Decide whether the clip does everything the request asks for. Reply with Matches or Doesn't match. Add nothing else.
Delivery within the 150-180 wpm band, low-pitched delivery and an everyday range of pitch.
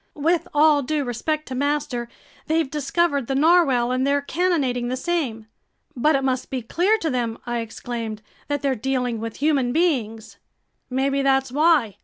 Doesn't match